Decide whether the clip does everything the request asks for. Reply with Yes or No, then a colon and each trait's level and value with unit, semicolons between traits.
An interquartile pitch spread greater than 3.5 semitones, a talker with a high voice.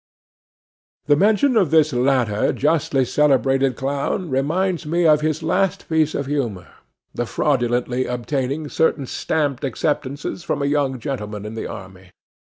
No: average, 4.0 semitones; medium, 140 Hz